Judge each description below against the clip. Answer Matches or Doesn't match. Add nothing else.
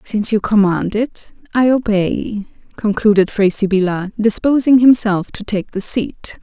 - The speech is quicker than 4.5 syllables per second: Doesn't match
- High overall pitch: Matches